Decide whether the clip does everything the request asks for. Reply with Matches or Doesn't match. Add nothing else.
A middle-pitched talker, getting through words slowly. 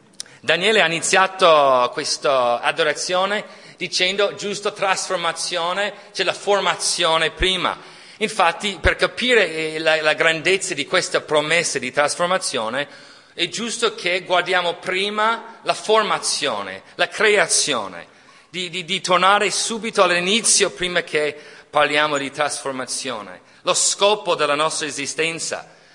Matches